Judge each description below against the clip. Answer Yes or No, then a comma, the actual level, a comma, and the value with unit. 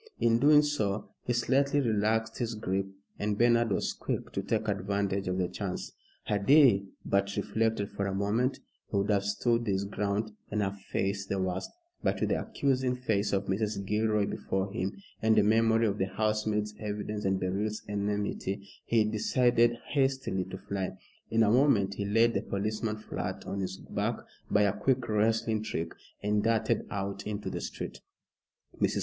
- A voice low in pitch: Yes, low, 105 Hz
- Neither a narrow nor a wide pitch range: No, narrow, 2.3 semitones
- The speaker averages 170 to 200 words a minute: Yes, average, 175 wpm